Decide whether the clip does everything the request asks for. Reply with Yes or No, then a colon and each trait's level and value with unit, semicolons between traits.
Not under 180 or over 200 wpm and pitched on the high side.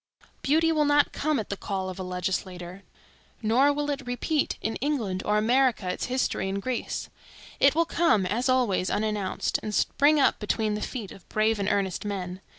Yes: average, 185 wpm; high, 215 Hz